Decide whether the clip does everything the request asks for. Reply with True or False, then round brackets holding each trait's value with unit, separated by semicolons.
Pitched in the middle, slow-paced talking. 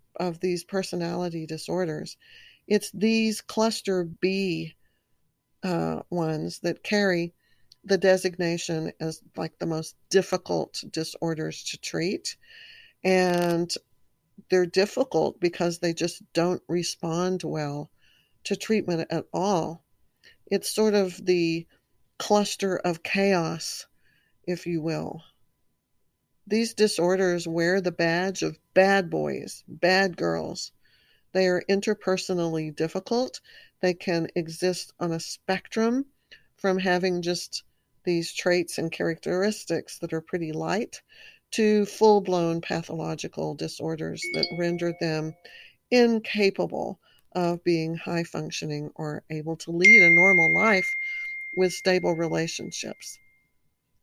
True (175 Hz; 110 wpm)